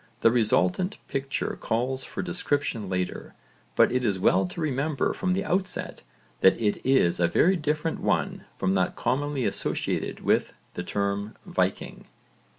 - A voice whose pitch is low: Yes, low, 130 Hz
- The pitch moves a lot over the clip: Yes, wide, 7.2 semitones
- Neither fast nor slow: Yes, average, 150 wpm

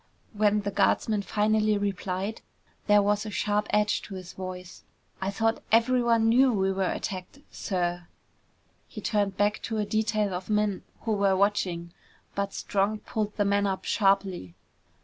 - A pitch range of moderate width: No, narrow, 1.9 semitones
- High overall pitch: Yes, high, 205 Hz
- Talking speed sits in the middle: Yes, average, 155 wpm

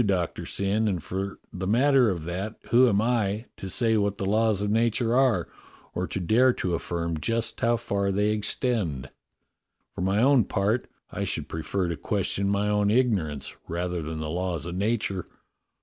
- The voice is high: No, low, 100 Hz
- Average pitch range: Yes, average, 4.0 semitones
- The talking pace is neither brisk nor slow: Yes, average, 180 wpm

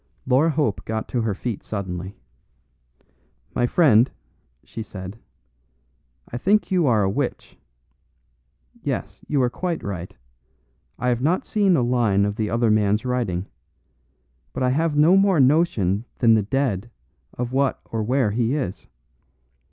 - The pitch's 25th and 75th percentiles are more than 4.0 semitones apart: Yes, average, 5.2 semitones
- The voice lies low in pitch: Yes, low, 120 Hz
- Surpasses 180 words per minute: No, average, 145 wpm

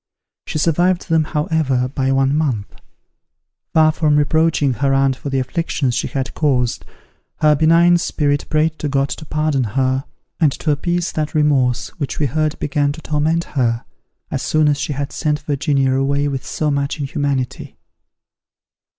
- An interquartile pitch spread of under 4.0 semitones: Yes, narrow, 2.5 semitones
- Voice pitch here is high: No, medium, 145 Hz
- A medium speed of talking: Yes, average, 160 wpm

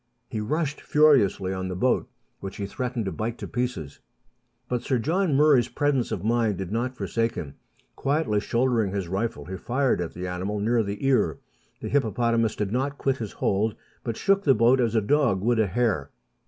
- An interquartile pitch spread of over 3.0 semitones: Yes, average, 4.6 semitones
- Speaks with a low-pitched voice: Yes, low, 115 Hz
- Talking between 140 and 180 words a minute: No, average, 195 wpm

